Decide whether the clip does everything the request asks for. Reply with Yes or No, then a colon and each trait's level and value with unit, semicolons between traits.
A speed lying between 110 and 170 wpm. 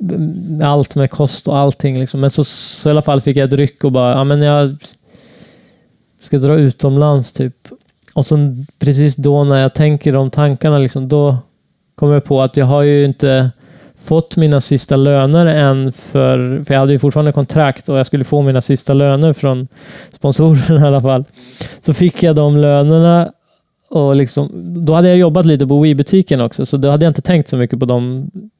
No: fast, 195 wpm